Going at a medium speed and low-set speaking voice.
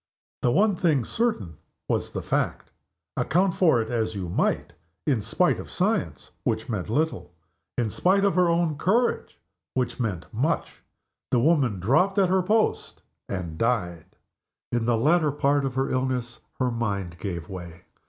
Yes: average, 160 wpm; low, 125 Hz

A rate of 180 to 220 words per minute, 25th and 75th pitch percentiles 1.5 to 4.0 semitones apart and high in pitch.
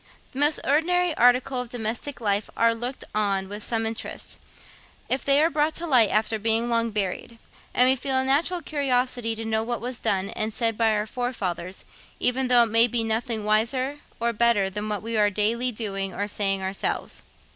Yes: average, 195 wpm; average, 3.2 semitones; high, 230 Hz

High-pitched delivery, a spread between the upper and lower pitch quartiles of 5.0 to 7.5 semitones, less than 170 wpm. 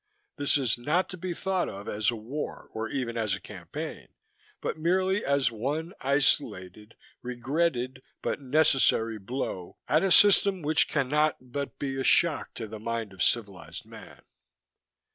No: low, 135 Hz; wide, 5.5 semitones; average, 155 wpm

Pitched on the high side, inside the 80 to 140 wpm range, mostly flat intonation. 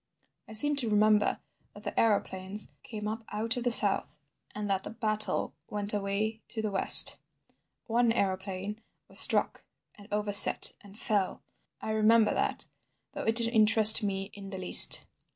No: high, 210 Hz; average, 155 wpm; narrow, 1.7 semitones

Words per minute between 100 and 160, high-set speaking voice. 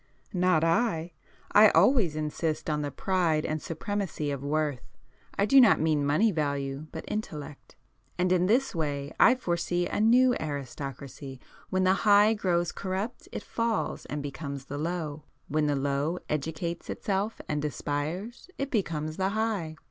No: average, 150 wpm; medium, 165 Hz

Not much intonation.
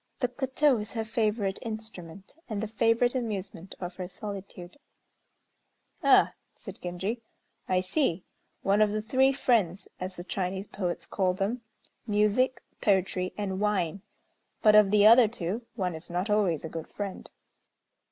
No: average, 3.3 semitones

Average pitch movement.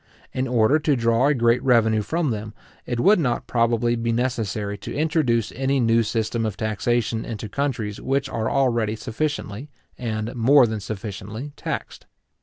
Yes: average, 3.4 semitones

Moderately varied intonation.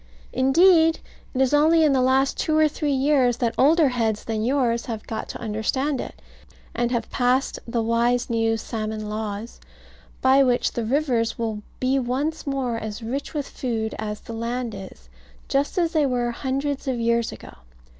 Yes: average, 3.3 semitones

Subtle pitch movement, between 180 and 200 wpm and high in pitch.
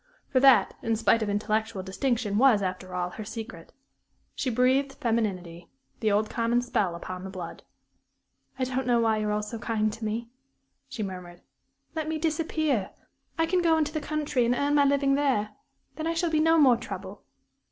No: average, 5.2 semitones; average, 185 wpm; high, 230 Hz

